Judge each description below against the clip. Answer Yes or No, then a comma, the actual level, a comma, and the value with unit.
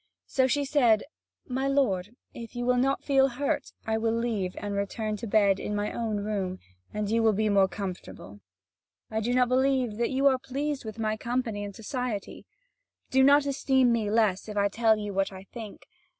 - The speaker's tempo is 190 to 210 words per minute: Yes, average, 195 wpm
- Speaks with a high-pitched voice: Yes, high, 225 Hz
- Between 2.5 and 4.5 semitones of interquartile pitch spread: Yes, average, 3.9 semitones